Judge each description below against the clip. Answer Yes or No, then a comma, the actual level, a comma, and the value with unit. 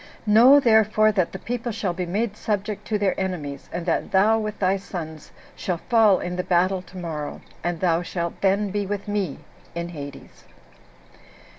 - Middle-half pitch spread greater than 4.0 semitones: No, average, 3.3 semitones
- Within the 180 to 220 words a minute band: No, average, 170 wpm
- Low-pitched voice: No, high, 190 Hz